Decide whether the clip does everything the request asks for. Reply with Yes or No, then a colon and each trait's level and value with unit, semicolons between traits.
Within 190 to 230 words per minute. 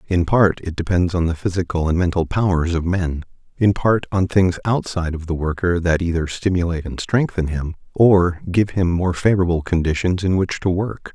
Yes: average, 195 wpm